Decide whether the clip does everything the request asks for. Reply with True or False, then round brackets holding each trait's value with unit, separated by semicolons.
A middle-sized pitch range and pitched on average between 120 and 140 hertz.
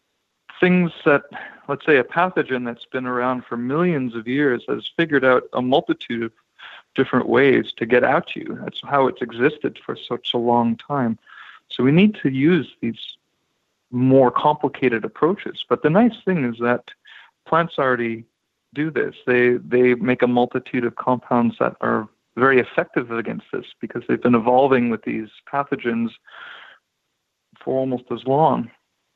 True (3.0 semitones; 125 Hz)